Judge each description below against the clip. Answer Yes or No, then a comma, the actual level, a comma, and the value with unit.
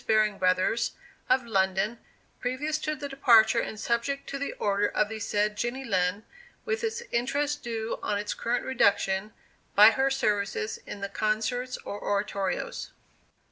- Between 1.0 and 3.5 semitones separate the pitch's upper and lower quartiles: No, average, 4.4 semitones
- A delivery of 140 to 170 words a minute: Yes, average, 150 wpm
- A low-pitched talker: No, high, 220 Hz